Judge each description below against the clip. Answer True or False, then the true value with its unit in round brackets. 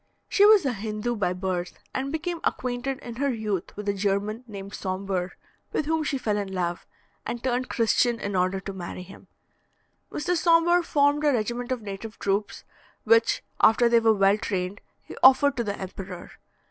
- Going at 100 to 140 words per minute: False (180 wpm)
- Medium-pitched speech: False (220 Hz)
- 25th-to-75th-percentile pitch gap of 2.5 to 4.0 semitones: False (5.3 semitones)